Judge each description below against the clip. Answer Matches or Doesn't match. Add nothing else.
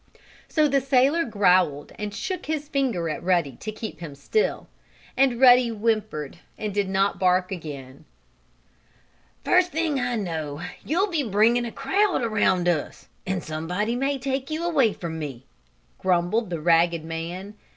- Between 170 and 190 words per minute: Doesn't match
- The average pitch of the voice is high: Matches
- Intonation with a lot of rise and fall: Matches